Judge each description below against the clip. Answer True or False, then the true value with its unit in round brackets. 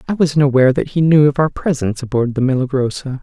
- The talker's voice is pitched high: False (140 Hz)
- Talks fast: True (225 wpm)